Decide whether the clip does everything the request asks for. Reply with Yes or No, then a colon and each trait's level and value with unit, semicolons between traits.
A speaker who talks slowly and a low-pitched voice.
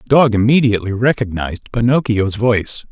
Yes: slow, 125 wpm; low, 115 Hz